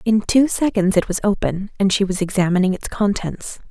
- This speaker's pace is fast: No, average, 195 wpm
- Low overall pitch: No, high, 200 Hz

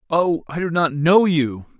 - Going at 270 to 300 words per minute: No, average, 200 wpm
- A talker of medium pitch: Yes, medium, 160 Hz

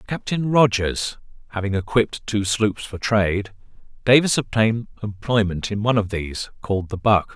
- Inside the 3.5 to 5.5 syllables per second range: Yes, 5.2 syllables/s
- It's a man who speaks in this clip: Yes, male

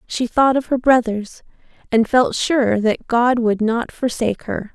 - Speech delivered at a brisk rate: No, average, 175 wpm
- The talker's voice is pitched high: Yes, high, 235 Hz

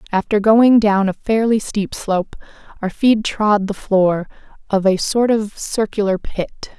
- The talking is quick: No, average, 160 wpm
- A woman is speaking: Yes, female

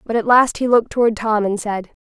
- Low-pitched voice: No, high, 220 Hz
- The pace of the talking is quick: Yes, fast, 265 wpm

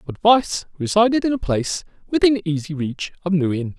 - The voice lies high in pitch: No, medium, 180 Hz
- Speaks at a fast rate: No, average, 190 wpm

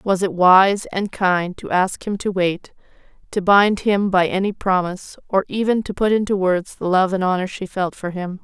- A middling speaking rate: No, fast, 215 wpm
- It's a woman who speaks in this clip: Yes, female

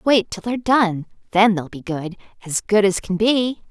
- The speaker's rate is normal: Yes, average, 195 wpm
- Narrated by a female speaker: Yes, female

